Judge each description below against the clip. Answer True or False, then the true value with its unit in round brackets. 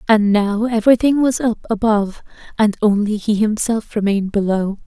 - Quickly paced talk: False (150 wpm)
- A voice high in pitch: True (215 Hz)